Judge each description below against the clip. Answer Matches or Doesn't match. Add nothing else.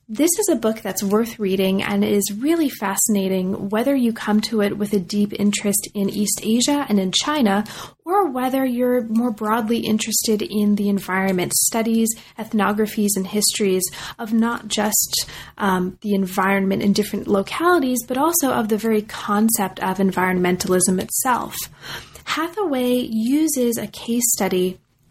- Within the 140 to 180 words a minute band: Matches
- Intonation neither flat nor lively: Matches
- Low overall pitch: Doesn't match